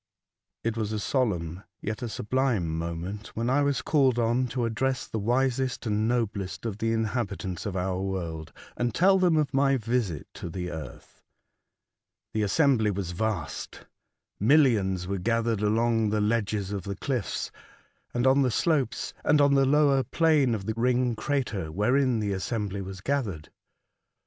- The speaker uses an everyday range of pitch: Yes, average, 4.9 semitones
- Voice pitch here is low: Yes, low, 115 Hz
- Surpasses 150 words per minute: Yes, average, 160 wpm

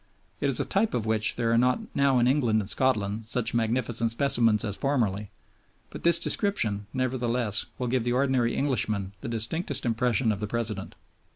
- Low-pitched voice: Yes, low, 120 Hz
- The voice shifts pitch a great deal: No, average, 3.0 semitones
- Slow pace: No, average, 180 wpm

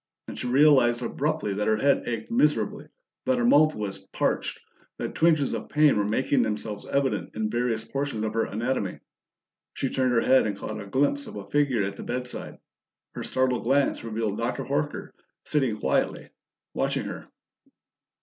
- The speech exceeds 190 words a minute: No, average, 175 wpm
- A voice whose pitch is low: Yes, low, 125 Hz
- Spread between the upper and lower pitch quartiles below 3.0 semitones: No, average, 4.7 semitones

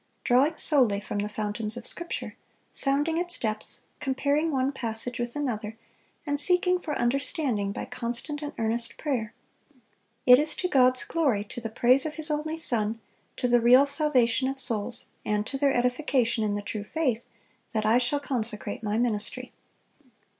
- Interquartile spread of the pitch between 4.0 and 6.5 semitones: Yes, average, 4.7 semitones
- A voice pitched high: Yes, very high, 250 Hz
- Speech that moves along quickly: No, average, 165 wpm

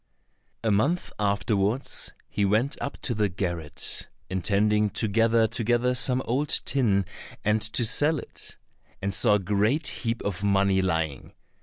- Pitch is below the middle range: Yes, low, 105 Hz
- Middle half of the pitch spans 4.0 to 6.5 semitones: No, average, 3.5 semitones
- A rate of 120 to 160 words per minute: Yes, average, 145 wpm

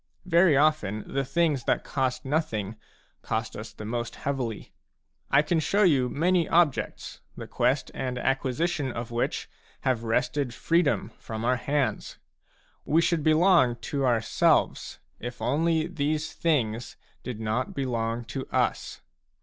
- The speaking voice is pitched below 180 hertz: Yes, low, 135 Hz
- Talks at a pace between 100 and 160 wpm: Yes, average, 140 wpm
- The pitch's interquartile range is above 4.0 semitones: Yes, average, 4.8 semitones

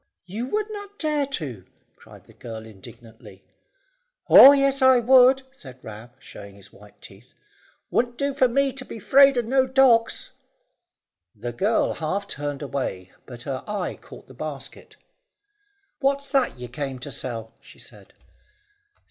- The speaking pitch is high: Yes, high, 210 Hz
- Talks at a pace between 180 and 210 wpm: No, average, 150 wpm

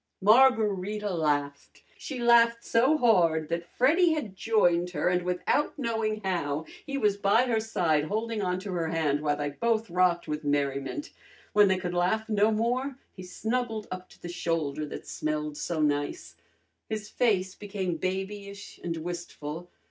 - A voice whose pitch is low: No, high, 190 Hz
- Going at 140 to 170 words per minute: Yes, average, 160 wpm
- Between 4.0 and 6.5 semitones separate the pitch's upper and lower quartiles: Yes, average, 5.1 semitones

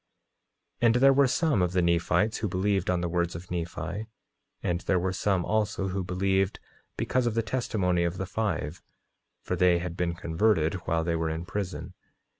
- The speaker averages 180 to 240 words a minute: Yes, average, 190 wpm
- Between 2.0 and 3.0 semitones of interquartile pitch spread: No, average, 3.4 semitones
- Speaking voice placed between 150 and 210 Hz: No, very low, 90 Hz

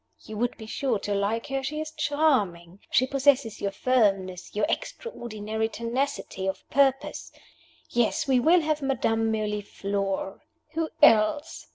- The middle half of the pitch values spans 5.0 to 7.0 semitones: Yes, average, 5.3 semitones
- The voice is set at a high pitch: Yes, high, 230 Hz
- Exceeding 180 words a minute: No, average, 140 wpm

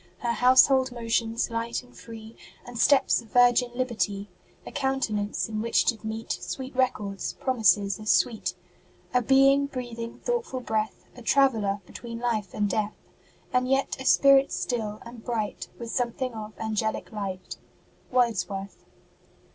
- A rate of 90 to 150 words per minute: Yes, average, 140 wpm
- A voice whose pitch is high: Yes, high, 230 Hz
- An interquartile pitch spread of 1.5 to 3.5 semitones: Yes, average, 2.9 semitones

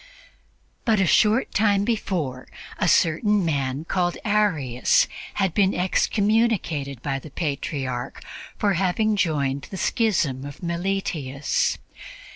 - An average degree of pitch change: No, wide, 6.6 semitones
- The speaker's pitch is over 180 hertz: No, medium, 175 Hz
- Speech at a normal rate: No, slow, 110 wpm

